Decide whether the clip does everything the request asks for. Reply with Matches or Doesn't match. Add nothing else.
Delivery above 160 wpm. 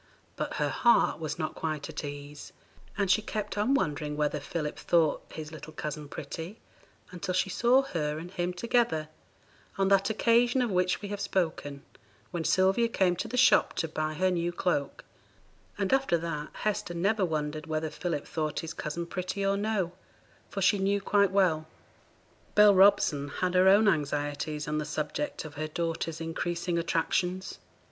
Matches